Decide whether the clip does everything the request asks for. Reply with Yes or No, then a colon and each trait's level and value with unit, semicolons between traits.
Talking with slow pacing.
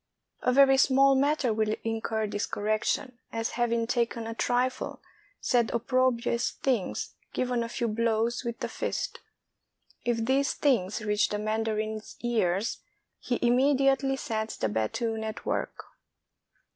Yes: slow, 130 wpm